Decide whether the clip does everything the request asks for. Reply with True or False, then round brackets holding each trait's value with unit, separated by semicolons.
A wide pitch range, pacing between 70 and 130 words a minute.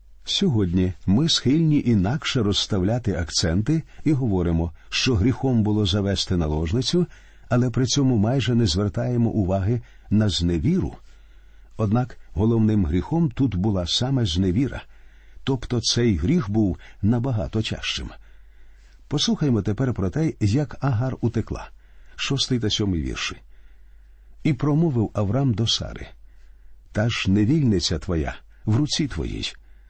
True (6.0 semitones; 115 wpm)